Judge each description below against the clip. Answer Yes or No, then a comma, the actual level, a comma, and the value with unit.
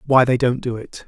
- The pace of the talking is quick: Yes, fast, 280 wpm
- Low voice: Yes, low, 125 Hz